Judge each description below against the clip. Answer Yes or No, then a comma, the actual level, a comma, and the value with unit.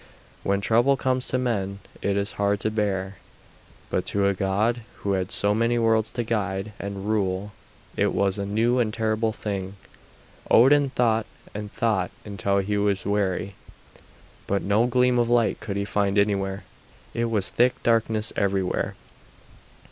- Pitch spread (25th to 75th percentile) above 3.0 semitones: No, narrow, 2.6 semitones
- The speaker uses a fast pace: No, average, 155 wpm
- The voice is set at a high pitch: No, low, 105 Hz